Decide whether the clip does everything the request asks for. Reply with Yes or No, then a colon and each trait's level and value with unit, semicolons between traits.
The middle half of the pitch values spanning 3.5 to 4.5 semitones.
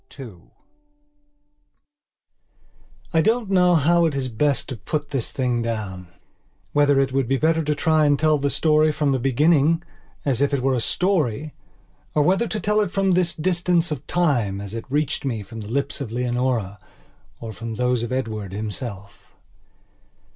No: wide, 5.4 semitones